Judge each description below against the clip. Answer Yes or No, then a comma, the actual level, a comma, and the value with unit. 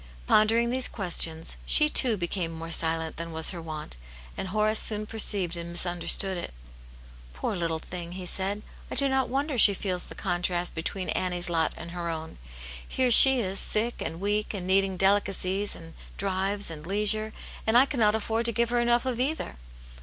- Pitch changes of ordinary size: Yes, average, 4.3 semitones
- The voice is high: Yes, high, 195 Hz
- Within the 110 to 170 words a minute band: No, average, 185 wpm